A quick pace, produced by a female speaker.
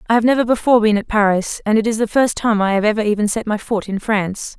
Yes: fast, 290 wpm; female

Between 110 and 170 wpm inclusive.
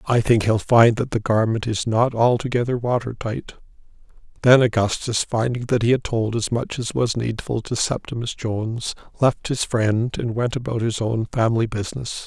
No: average, 180 wpm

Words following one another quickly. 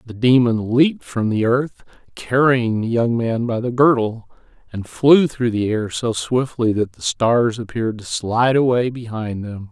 No: average, 180 wpm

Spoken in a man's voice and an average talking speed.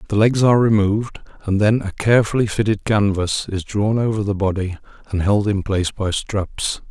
Yes: male; average, 180 wpm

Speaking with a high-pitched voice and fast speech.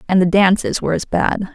Yes: high, 195 Hz; fast, 235 wpm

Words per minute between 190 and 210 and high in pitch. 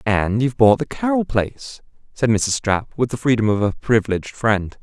No: average, 200 wpm; low, 115 Hz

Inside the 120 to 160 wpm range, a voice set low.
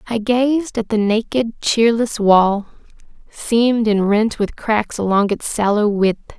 No: average, 150 wpm; high, 220 Hz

